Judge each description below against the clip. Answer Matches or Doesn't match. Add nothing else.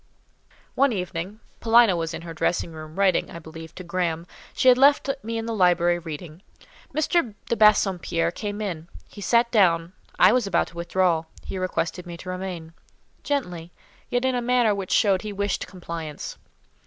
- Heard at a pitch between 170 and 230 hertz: Matches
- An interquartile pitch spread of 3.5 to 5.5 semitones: Matches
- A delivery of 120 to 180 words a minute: Matches